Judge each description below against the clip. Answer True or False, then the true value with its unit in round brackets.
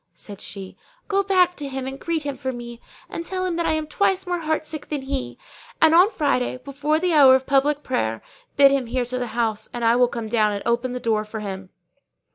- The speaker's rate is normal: False (240 wpm)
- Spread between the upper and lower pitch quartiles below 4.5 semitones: False (4.9 semitones)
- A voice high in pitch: True (265 Hz)